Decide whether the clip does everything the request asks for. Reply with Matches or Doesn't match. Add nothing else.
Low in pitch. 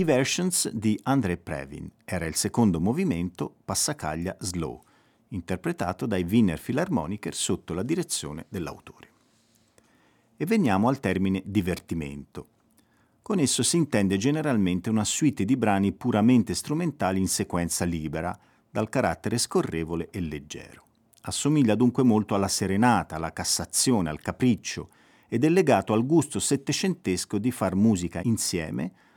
Matches